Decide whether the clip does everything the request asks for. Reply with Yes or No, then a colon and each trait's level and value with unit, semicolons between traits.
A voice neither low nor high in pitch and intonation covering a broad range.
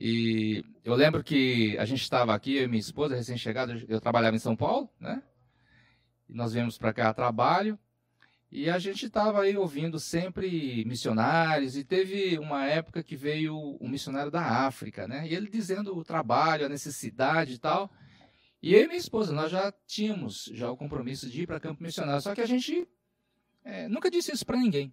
Yes: medium, 145 Hz; wide, 7.3 semitones